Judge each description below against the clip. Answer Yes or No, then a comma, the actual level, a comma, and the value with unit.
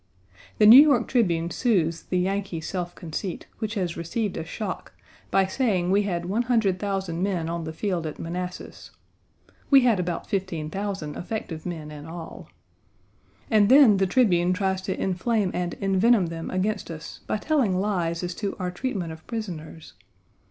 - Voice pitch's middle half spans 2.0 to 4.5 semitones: Yes, average, 3.6 semitones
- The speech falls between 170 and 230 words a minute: No, average, 160 wpm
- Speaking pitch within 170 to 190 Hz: Yes, medium, 185 Hz